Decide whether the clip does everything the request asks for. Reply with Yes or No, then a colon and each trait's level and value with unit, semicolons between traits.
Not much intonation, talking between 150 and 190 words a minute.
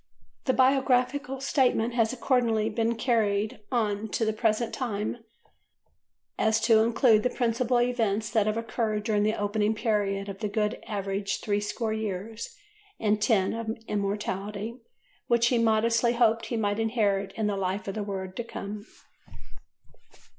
Yes: narrow, 2.1 semitones; average, 155 wpm